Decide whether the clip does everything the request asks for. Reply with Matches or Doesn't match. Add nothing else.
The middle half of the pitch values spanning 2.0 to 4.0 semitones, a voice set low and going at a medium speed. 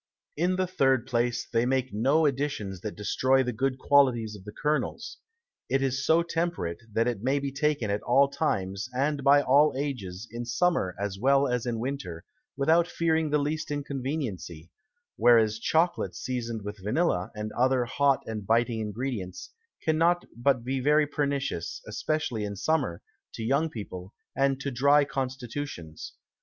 Doesn't match